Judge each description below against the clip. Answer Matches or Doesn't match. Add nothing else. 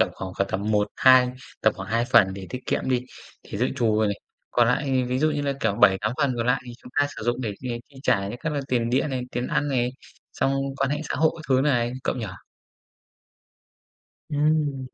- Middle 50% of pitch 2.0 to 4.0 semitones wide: Matches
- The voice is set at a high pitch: Doesn't match